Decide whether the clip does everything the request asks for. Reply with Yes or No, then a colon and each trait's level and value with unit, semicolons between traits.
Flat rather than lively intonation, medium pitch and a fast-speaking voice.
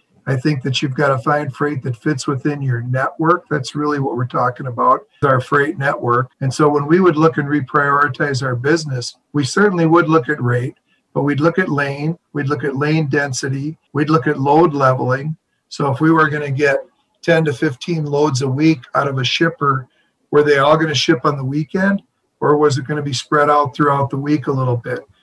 Yes: narrow, 2.3 semitones; medium, 145 Hz; fast, 220 wpm